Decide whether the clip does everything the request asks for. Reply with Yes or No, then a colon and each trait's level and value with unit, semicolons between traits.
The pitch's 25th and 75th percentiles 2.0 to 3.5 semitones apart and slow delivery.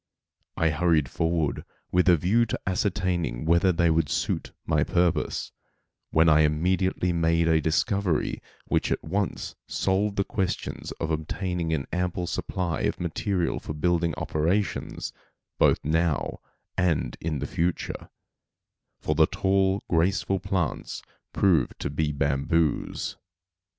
Yes: average, 2.8 semitones; slow, 130 wpm